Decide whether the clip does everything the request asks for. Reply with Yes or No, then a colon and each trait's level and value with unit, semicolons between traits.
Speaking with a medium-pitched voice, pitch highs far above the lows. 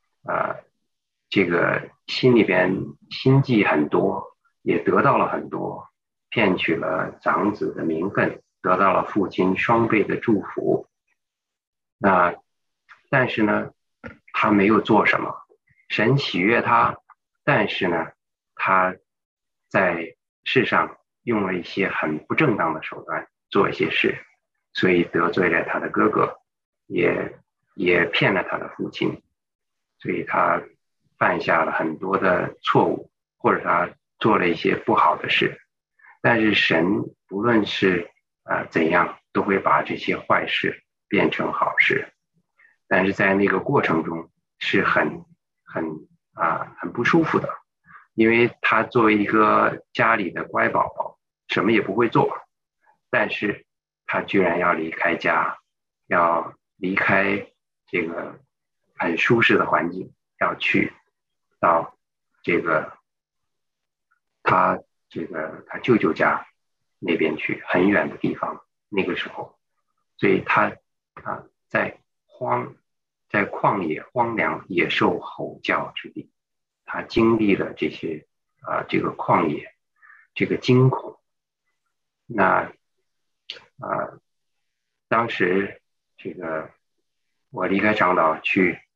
No: very low, 95 Hz; wide, 6.2 semitones